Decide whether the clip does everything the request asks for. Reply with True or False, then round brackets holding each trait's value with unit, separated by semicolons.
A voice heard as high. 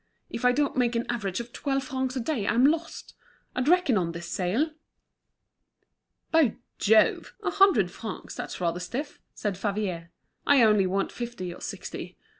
True (235 Hz)